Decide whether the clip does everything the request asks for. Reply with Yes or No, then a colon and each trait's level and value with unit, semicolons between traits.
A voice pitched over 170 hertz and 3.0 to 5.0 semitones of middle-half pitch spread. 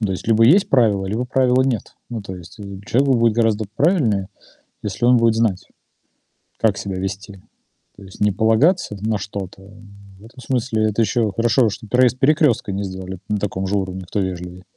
No: low, 105 Hz; average, 3.6 semitones